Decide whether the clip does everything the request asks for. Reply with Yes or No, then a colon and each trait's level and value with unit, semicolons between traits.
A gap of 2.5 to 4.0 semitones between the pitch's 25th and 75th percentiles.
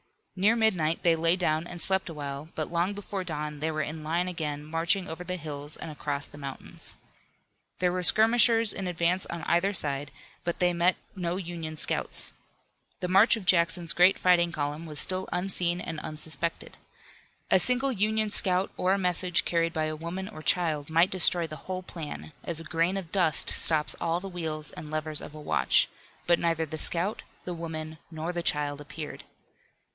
Yes: average, 2.8 semitones